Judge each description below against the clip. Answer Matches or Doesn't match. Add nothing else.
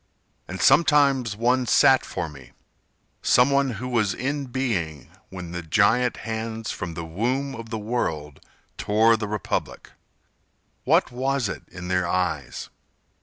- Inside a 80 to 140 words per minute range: Matches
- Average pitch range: Doesn't match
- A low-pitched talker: Matches